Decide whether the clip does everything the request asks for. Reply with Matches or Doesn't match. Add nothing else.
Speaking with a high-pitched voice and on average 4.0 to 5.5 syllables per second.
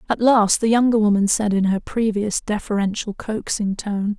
Matches